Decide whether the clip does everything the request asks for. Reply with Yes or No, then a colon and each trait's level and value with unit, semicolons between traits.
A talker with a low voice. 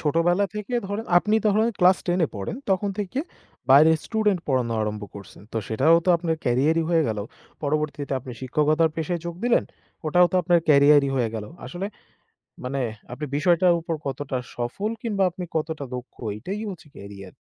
No: medium, 160 Hz